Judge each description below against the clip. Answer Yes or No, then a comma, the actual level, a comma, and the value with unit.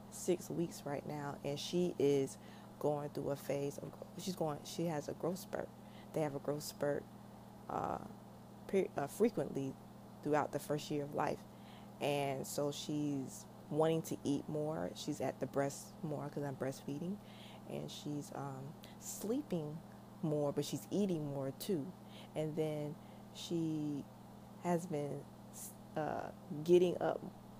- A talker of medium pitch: Yes, medium, 145 Hz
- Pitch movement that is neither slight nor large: No, narrow, 2.3 semitones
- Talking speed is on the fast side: No, average, 145 wpm